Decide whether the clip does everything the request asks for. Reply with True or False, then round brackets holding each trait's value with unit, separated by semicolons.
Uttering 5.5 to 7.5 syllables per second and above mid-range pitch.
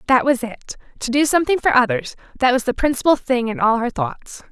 True (6.0 syllables/s; 265 Hz)